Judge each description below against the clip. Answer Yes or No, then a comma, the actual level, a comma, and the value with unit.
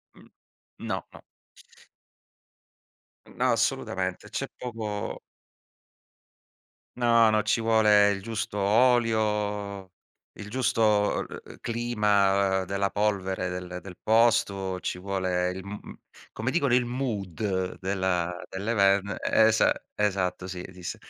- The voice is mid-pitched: No, low, 100 Hz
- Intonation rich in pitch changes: No, average, 2.8 semitones